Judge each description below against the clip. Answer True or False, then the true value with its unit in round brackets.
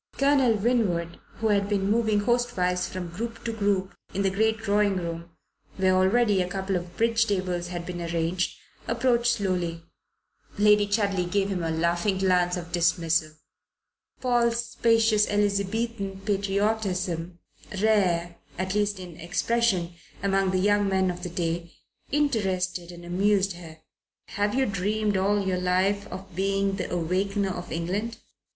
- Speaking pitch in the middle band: False (195 Hz)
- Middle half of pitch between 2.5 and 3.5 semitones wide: True (2.8 semitones)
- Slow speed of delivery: False (145 wpm)